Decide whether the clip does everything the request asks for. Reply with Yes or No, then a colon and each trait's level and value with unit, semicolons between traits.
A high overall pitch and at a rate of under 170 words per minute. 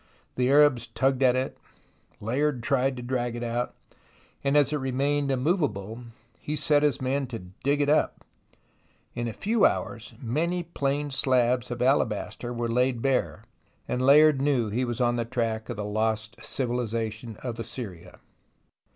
No: low, 125 Hz; average, 160 wpm